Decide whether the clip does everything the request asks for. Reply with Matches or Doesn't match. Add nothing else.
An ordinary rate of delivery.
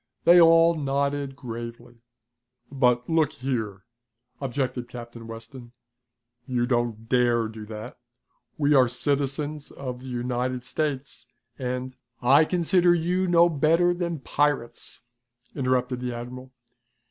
Doesn't match